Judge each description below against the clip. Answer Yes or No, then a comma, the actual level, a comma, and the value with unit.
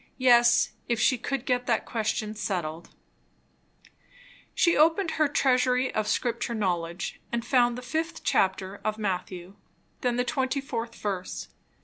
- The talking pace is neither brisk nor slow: No, slow, 130 wpm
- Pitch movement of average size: Yes, average, 4.1 semitones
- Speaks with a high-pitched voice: Yes, high, 235 Hz